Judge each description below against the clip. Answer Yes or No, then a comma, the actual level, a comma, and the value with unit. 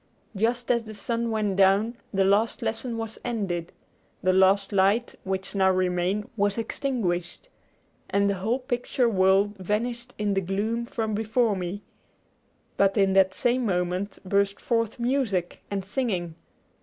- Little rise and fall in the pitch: No, average, 3.3 semitones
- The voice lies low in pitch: No, high, 205 Hz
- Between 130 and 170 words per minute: Yes, average, 145 wpm